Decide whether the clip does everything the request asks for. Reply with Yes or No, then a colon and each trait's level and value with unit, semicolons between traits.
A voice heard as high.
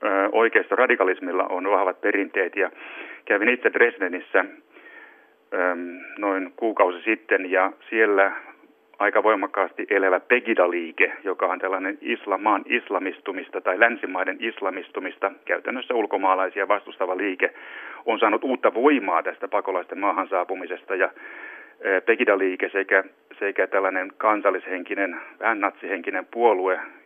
Yes: very high, 340 Hz